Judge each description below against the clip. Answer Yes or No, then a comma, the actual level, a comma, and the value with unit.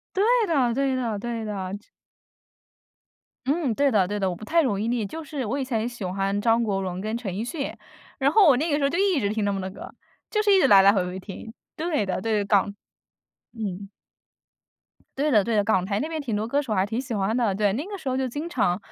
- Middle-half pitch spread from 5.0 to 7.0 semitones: Yes, wide, 5.6 semitones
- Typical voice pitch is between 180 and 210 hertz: No, high, 225 Hz